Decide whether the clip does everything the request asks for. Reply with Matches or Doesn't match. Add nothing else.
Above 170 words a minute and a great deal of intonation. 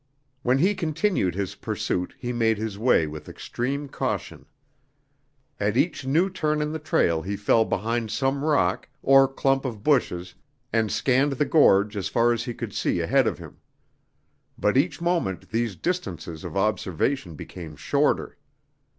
Doesn't match